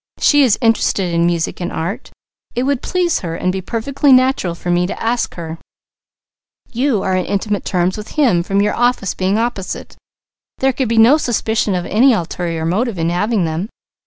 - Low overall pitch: No, high, 205 Hz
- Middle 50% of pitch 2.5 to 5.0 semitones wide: No, wide, 5.5 semitones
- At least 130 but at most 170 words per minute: No, average, 190 wpm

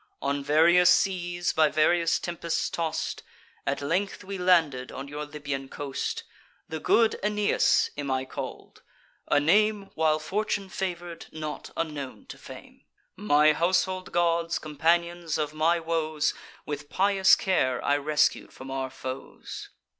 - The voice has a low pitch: No, medium, 160 Hz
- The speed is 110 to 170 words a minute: Yes, slow, 135 wpm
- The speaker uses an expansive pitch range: No, average, 3.5 semitones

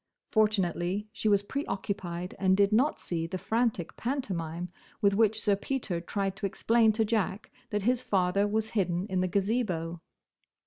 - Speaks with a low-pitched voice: No, high, 200 Hz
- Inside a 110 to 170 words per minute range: Yes, average, 160 wpm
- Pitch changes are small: No, average, 3.4 semitones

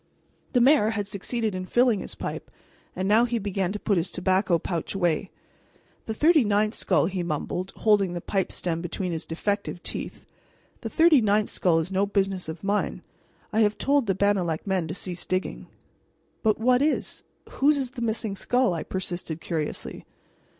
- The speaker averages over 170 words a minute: Yes, average, 180 wpm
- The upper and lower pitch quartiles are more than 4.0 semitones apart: No, average, 3.7 semitones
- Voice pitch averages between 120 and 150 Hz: No, high, 200 Hz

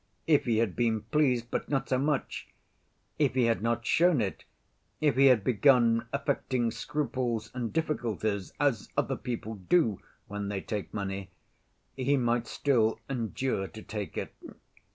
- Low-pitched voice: Yes, low, 120 Hz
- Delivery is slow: No, average, 155 wpm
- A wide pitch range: No, average, 3.7 semitones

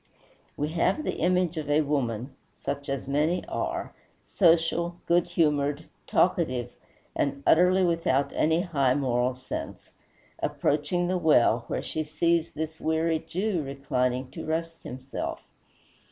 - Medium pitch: Yes, medium, 155 Hz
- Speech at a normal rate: No, slow, 130 wpm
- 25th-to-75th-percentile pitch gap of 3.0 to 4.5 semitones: Yes, average, 3.6 semitones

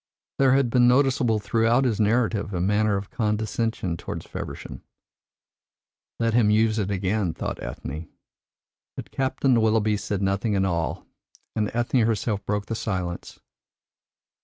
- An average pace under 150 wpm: Yes, slow, 135 wpm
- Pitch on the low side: Yes, low, 110 Hz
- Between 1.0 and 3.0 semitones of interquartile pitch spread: Yes, narrow, 2.6 semitones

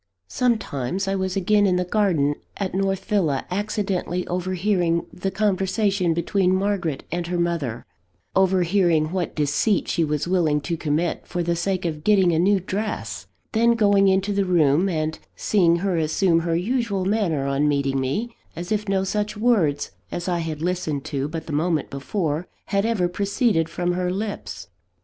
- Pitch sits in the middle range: Yes, medium, 180 Hz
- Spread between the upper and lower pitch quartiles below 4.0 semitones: Yes, average, 3.5 semitones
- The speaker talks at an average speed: Yes, average, 170 wpm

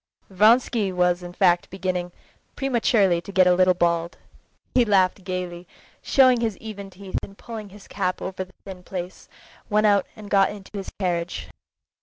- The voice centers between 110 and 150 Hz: No, high, 190 Hz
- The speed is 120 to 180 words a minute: Yes, average, 165 wpm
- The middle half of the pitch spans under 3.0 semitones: Yes, narrow, 2.5 semitones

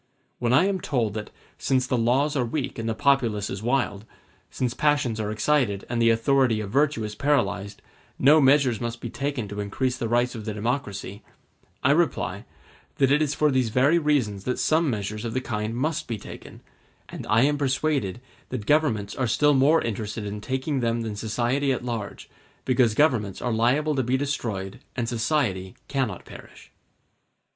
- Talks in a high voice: No, low, 120 Hz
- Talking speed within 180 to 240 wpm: Yes, average, 185 wpm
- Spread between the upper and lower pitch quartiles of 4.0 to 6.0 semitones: Yes, average, 4.3 semitones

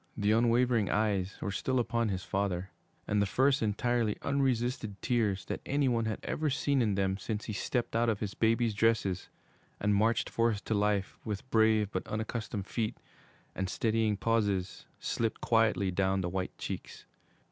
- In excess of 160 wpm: Yes, average, 170 wpm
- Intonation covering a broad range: No, narrow, 2.6 semitones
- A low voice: Yes, low, 110 Hz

